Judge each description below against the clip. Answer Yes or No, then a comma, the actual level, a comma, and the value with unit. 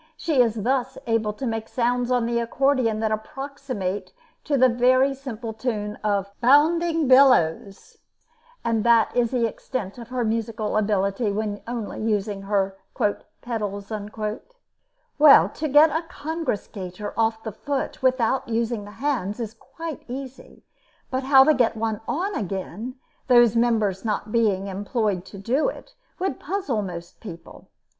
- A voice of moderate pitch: No, high, 230 Hz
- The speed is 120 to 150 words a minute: Yes, average, 145 wpm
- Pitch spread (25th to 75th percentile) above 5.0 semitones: No, average, 4.0 semitones